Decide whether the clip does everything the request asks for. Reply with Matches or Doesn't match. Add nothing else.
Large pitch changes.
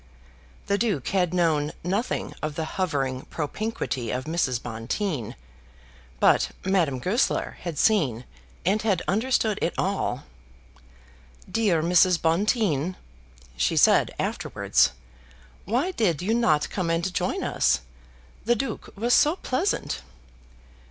Matches